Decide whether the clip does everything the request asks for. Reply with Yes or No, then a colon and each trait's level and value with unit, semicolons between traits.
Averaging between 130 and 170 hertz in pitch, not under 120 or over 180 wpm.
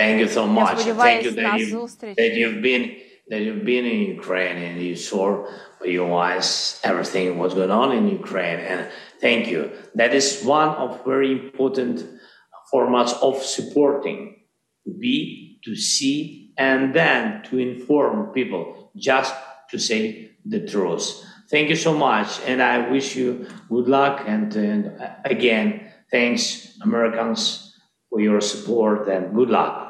Yes: low, 135 Hz; average, 150 wpm